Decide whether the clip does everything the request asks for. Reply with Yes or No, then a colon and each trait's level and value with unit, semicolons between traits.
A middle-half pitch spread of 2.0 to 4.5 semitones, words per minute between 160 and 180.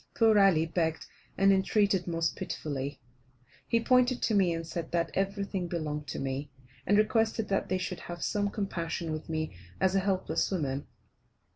Yes: average, 3.8 semitones; average, 165 wpm